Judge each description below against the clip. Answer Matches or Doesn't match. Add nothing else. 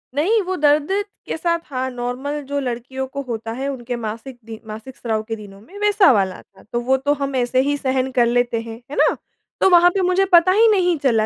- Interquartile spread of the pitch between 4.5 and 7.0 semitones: Matches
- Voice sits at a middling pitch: Doesn't match